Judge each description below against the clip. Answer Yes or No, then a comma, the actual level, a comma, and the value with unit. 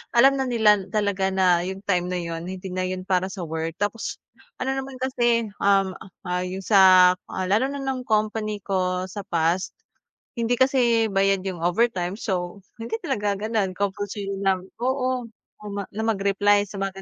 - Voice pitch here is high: Yes, high, 200 Hz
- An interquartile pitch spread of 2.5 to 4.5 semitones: Yes, average, 3.4 semitones